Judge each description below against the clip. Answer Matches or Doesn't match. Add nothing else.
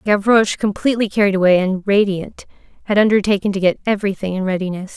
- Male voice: Doesn't match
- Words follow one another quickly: Doesn't match